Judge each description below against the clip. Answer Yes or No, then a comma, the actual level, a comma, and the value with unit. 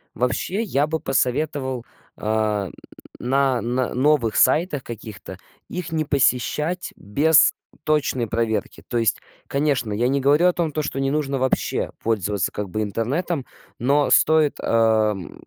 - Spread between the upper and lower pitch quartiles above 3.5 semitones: Yes, average, 4.8 semitones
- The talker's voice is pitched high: No, low, 130 Hz